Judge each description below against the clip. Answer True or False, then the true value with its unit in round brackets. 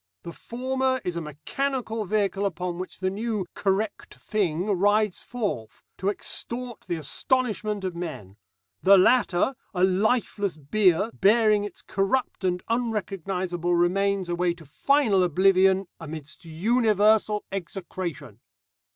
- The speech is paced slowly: True (120 wpm)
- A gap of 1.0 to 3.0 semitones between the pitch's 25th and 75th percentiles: False (3.7 semitones)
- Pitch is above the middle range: True (195 Hz)